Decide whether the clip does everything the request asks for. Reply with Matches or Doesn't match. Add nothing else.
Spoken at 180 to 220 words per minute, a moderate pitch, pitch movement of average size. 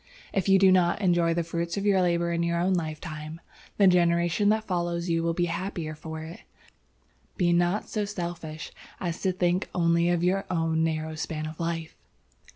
Doesn't match